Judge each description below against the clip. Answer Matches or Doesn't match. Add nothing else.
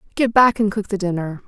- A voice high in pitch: Matches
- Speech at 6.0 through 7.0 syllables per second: Matches